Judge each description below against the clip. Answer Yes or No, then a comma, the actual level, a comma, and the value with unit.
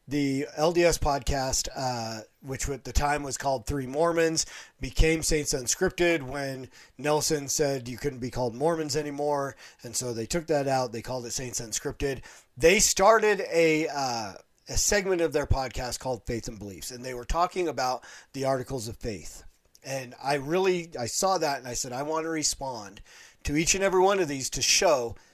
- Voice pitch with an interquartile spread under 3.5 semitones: No, average, 4.0 semitones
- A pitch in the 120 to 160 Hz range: Yes, medium, 140 Hz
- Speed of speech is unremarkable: Yes, average, 185 wpm